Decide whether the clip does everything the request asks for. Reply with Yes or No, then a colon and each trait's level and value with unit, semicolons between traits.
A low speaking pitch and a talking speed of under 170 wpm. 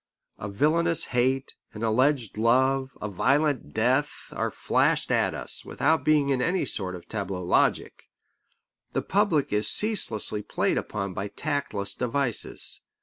Yes: low, 130 Hz; average, 140 wpm